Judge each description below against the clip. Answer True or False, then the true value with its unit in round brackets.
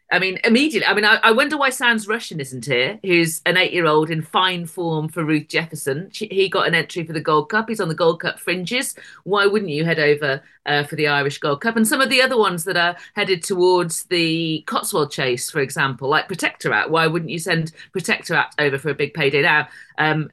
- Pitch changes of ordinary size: True (4.5 semitones)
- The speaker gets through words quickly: True (230 wpm)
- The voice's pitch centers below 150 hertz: False (170 Hz)